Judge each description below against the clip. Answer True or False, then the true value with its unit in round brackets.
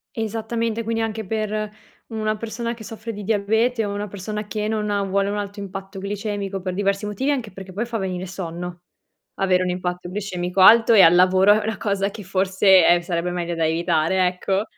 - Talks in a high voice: True (200 Hz)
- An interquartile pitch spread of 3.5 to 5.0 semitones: False (2.8 semitones)